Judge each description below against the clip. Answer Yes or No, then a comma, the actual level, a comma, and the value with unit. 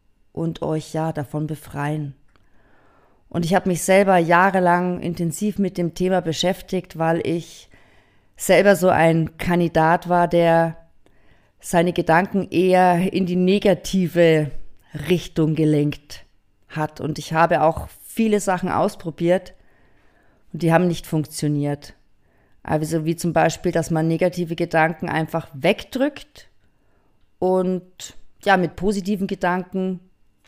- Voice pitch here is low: No, medium, 170 Hz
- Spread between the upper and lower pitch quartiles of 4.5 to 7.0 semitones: No, average, 2.8 semitones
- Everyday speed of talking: No, slow, 120 wpm